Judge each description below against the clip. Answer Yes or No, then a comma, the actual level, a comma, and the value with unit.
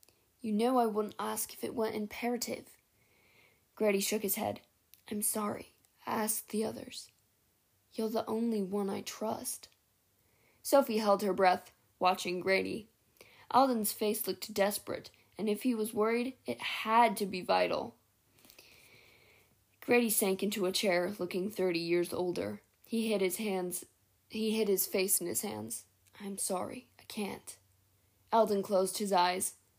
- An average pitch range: Yes, average, 3.2 semitones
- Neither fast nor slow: Yes, average, 145 wpm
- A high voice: Yes, high, 205 Hz